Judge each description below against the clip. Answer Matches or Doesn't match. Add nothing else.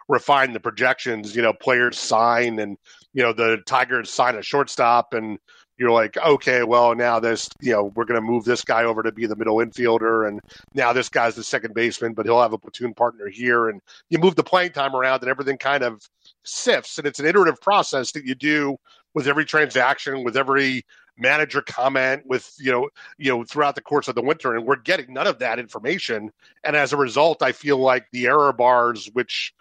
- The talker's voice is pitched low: Matches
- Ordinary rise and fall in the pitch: Matches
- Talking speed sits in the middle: Doesn't match